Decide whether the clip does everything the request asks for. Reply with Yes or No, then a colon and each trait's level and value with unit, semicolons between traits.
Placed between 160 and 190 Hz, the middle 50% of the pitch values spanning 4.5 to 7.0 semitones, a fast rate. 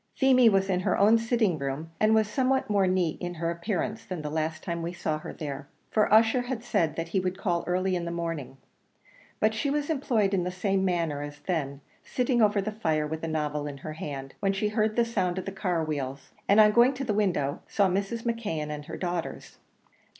Yes: medium, 185 Hz; wide, 5.4 semitones; fast, 225 wpm